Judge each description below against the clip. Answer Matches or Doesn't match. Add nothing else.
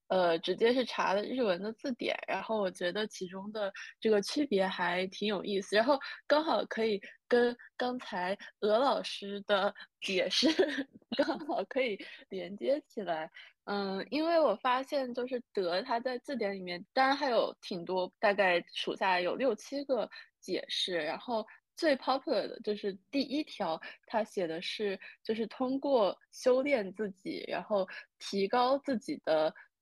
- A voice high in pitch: Matches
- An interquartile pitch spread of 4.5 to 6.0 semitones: Matches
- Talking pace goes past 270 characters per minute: Doesn't match